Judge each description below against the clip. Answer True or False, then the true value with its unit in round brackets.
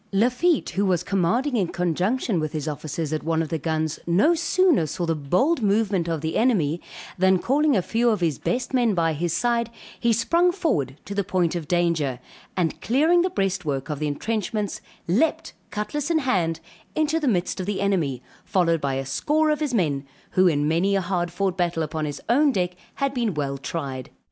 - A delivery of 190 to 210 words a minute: True (200 wpm)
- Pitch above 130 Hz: True (185 Hz)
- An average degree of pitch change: False (7.0 semitones)